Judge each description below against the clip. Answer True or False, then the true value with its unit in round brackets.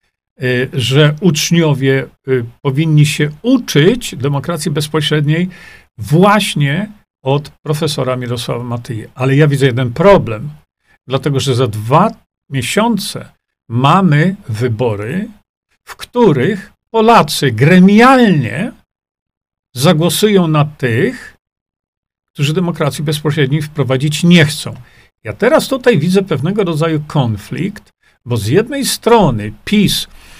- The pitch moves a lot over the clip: True (6.0 semitones)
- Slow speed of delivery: True (95 wpm)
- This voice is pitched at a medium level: True (155 Hz)